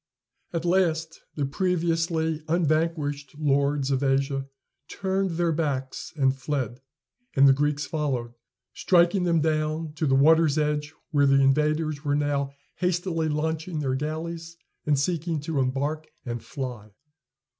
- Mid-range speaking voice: Yes, medium, 150 Hz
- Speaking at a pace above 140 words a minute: No, slow, 135 wpm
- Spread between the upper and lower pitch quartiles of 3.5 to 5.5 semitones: No, average, 2.8 semitones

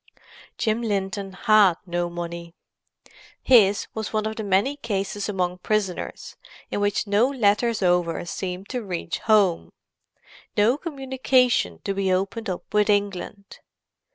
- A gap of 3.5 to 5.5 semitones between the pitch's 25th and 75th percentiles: No, average, 3.0 semitones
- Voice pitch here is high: Yes, high, 205 Hz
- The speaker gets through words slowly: Yes, slow, 125 wpm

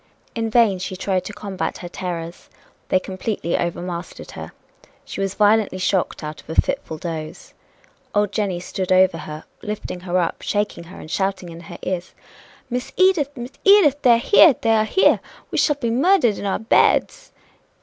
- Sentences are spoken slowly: No, average, 180 wpm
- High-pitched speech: Yes, high, 195 Hz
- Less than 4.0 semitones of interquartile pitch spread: No, average, 4.5 semitones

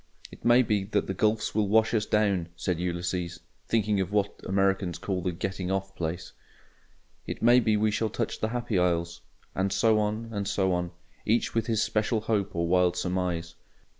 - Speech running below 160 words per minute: No, average, 190 wpm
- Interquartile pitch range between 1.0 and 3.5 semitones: Yes, average, 3.2 semitones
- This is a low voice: Yes, low, 100 Hz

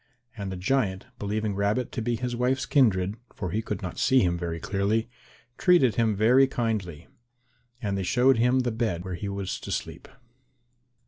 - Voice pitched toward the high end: No, low, 110 Hz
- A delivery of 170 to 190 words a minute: Yes, average, 180 wpm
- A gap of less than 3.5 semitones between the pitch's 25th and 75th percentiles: No, average, 4.2 semitones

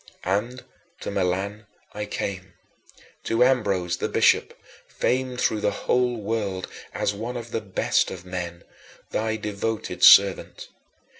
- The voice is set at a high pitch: No, low, 105 Hz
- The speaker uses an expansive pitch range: No, average, 3.2 semitones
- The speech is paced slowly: Yes, slow, 130 wpm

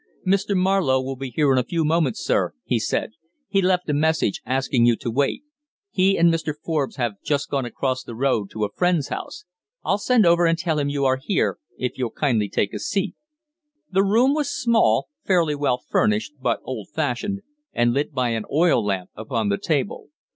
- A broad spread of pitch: Yes, wide, 6.3 semitones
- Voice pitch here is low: No, medium, 145 Hz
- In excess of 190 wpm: Yes, average, 200 wpm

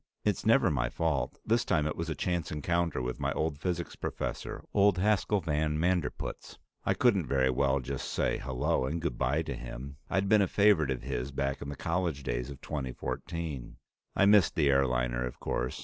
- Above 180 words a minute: Yes, average, 195 wpm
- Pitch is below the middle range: Yes, very low, 75 Hz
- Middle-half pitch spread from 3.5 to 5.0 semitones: Yes, average, 4.6 semitones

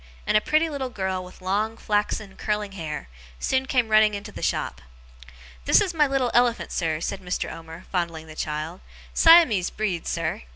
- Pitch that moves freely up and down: Yes, wide, 5.7 semitones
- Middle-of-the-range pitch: No, high, 205 Hz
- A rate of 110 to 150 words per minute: No, average, 175 wpm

